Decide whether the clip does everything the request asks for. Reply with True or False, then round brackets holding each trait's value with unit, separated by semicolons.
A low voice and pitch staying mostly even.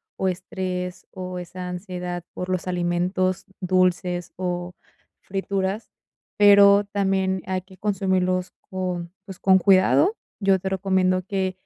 False (185 Hz; 1.1 semitones)